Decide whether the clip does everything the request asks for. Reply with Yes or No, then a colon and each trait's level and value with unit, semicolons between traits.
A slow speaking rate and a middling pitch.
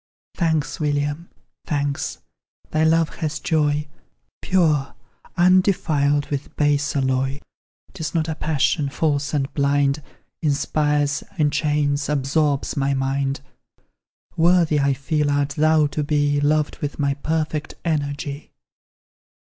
Yes: slow, 110 wpm; medium, 145 Hz